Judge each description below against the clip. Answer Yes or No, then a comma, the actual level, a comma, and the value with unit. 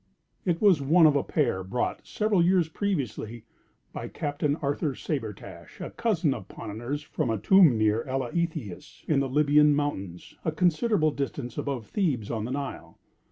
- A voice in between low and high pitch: Yes, medium, 145 Hz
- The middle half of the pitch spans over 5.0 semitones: Yes, wide, 5.5 semitones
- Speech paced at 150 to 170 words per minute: Yes, average, 160 wpm